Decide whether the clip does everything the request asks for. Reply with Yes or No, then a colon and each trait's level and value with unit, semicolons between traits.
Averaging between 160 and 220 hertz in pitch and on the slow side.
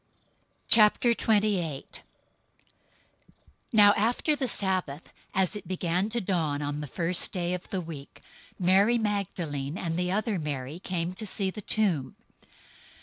Yes: medium, 185 Hz; slow, 130 wpm